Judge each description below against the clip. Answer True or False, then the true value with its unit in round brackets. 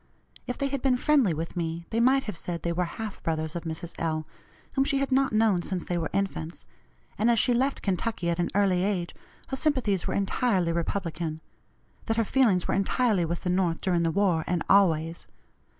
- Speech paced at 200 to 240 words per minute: True (205 wpm)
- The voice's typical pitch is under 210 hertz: True (190 Hz)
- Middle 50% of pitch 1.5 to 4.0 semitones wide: False (5.4 semitones)